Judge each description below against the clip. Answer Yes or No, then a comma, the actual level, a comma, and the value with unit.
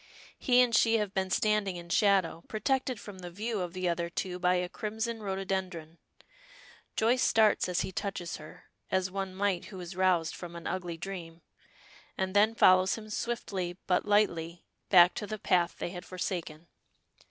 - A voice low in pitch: No, medium, 185 Hz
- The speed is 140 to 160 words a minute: No, average, 175 wpm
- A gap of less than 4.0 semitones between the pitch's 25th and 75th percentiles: Yes, average, 3.0 semitones